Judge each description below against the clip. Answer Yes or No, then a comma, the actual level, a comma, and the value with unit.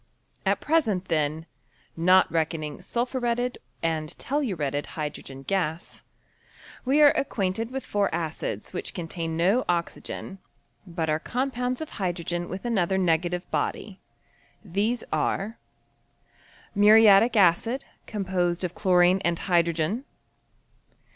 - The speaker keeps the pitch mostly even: No, average, 5.2 semitones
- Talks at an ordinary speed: No, slow, 100 wpm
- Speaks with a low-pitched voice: No, medium, 185 Hz